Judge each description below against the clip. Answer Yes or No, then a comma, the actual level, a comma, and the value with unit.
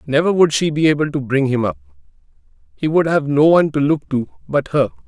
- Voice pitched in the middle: Yes, medium, 150 Hz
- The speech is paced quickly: Yes, fast, 215 wpm